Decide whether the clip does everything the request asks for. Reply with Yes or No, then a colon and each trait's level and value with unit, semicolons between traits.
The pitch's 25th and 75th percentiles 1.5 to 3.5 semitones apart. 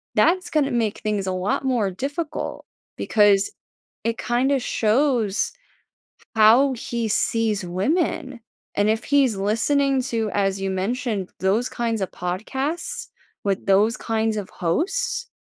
No: average, 5.0 semitones